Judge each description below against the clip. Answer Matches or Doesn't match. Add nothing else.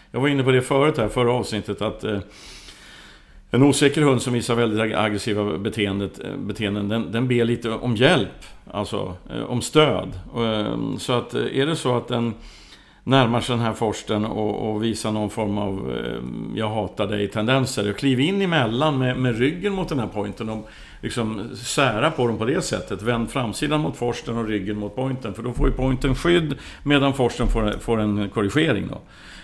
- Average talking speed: Matches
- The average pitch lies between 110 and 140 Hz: Matches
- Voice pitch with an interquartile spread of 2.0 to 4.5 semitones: Matches